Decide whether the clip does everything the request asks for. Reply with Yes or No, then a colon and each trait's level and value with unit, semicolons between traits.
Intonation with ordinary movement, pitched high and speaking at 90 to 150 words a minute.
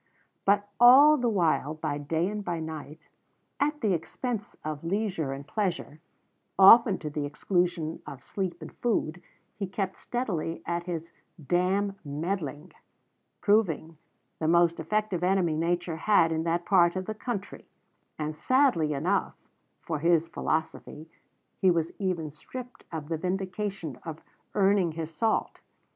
No: average, 4.0 semitones; medium, 175 Hz; average, 140 wpm